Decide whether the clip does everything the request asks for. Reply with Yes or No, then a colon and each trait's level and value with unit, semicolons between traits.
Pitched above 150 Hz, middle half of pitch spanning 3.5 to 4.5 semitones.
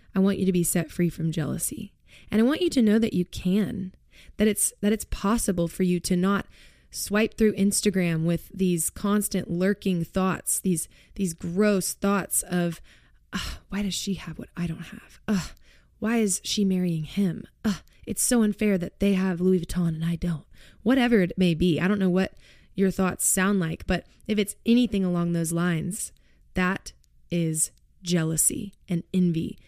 No: medium, 185 Hz; average, 2.9 semitones